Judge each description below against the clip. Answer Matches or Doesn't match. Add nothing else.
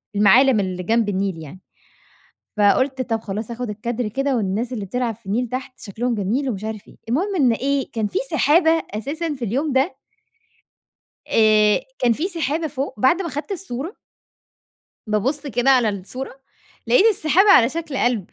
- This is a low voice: Doesn't match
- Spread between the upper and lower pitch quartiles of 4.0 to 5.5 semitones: Matches